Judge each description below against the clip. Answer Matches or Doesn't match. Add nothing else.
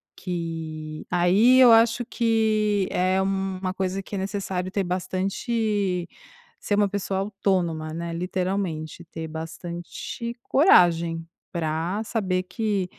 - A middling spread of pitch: Matches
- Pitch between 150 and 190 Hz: Matches